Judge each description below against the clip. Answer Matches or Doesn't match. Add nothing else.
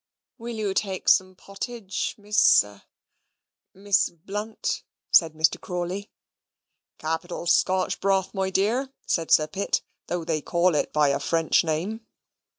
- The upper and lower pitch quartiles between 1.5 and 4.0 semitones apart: Matches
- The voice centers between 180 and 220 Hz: Matches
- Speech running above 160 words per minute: Doesn't match